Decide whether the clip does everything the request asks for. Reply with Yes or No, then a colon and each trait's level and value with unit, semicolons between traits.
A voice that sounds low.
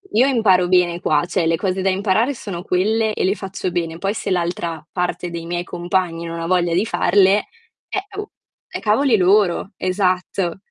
No: medium, 185 Hz